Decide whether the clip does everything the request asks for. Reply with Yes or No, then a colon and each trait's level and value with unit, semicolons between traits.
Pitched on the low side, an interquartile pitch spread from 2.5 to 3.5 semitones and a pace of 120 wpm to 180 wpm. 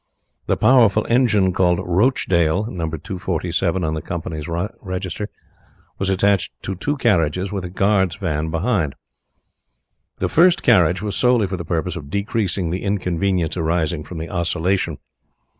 Yes: very low, 90 Hz; average, 3.2 semitones; average, 140 wpm